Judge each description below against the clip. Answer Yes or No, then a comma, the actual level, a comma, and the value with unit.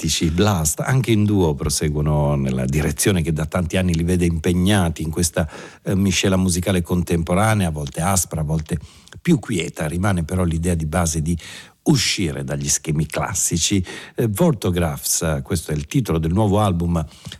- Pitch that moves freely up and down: No, average, 3.1 semitones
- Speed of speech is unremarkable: Yes, average, 160 wpm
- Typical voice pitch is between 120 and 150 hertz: No, very low, 85 Hz